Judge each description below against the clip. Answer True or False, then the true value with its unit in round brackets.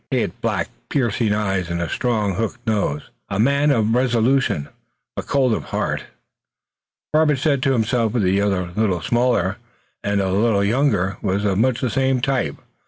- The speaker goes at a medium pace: True (170 wpm)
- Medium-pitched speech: False (110 Hz)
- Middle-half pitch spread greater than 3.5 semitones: True (4.6 semitones)